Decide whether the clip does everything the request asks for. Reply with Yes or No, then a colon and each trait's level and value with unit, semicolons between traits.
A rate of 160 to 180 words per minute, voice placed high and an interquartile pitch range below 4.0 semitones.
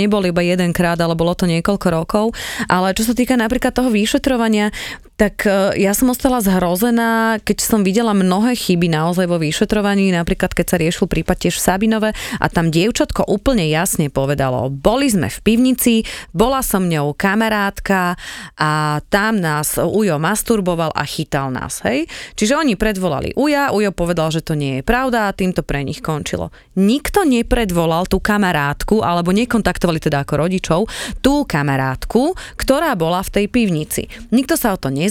No: fast, 165 wpm; high, 195 Hz; average, 5.0 semitones